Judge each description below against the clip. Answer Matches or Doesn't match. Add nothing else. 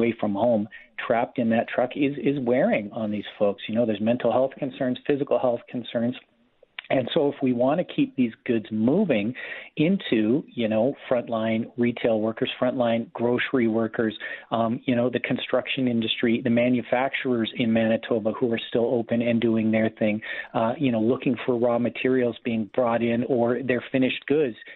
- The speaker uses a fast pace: Doesn't match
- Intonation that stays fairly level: Matches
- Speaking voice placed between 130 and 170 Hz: Doesn't match